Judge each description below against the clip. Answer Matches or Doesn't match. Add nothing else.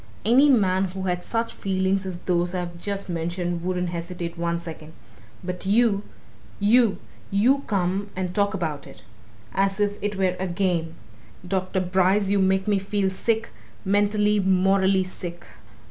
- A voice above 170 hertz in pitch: Matches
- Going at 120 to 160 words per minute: Matches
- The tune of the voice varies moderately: Doesn't match